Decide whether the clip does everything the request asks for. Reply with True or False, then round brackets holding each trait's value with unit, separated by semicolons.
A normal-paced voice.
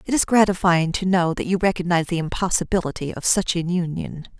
True (190 wpm)